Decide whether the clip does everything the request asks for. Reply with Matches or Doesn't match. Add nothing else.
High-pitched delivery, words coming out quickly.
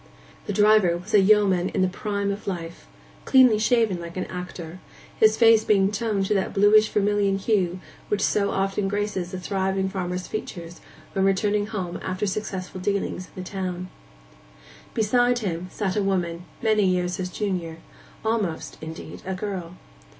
Doesn't match